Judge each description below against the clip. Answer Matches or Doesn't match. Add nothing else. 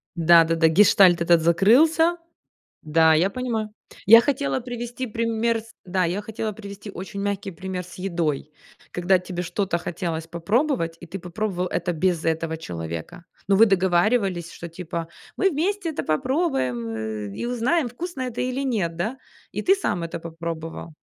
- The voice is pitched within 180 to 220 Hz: Matches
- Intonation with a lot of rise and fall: Matches